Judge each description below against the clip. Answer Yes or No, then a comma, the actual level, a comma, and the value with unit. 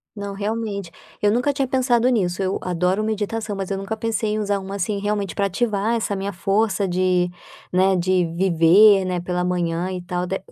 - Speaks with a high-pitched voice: Yes, high, 195 Hz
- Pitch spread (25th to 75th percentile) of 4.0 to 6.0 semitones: No, average, 2.8 semitones